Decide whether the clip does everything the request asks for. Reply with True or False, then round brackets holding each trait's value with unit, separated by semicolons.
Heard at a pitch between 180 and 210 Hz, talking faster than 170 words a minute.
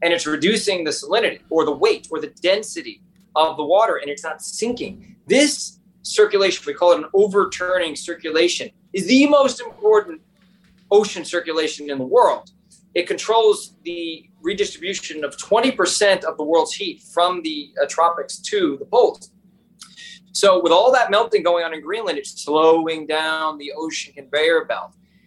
False (190 Hz; 160 wpm)